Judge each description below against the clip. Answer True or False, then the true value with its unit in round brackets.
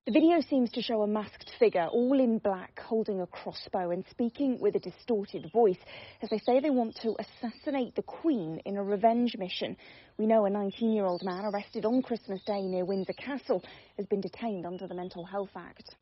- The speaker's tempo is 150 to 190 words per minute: False (205 wpm)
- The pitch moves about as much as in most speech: True (3.9 semitones)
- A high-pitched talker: True (215 Hz)